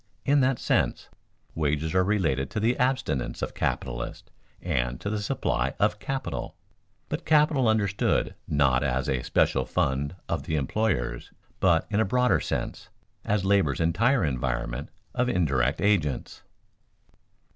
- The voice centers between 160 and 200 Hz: No, very low, 90 Hz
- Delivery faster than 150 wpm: No, slow, 135 wpm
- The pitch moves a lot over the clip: Yes, wide, 8.5 semitones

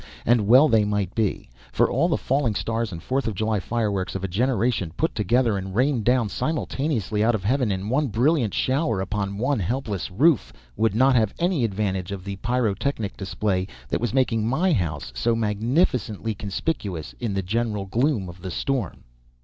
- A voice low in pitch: Yes, low, 110 Hz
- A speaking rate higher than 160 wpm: Yes, average, 180 wpm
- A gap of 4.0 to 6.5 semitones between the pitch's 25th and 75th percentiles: Yes, average, 4.5 semitones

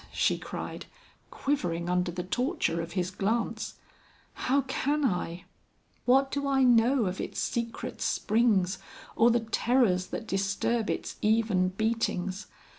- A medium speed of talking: No, slow, 130 wpm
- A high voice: Yes, high, 225 Hz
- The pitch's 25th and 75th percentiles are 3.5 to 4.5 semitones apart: No, average, 5.1 semitones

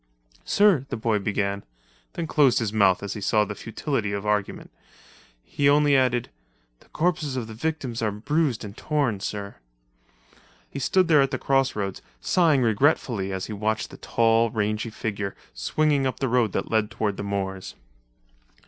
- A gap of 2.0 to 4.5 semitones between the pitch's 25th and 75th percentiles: No, average, 5.1 semitones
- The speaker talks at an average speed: Yes, average, 165 wpm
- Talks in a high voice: No, low, 115 Hz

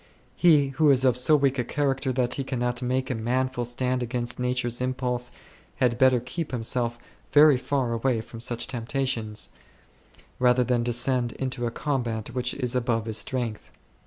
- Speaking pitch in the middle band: No, low, 125 Hz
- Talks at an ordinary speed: Yes, average, 165 wpm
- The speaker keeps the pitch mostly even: Yes, narrow, 1.6 semitones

